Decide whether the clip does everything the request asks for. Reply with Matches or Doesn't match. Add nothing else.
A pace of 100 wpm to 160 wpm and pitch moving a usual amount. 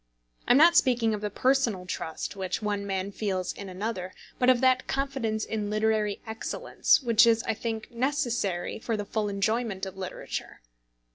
Doesn't match